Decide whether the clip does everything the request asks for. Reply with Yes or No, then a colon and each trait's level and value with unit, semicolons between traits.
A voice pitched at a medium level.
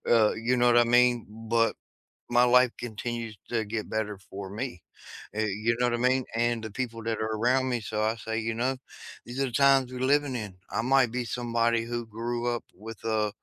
No: low, 115 Hz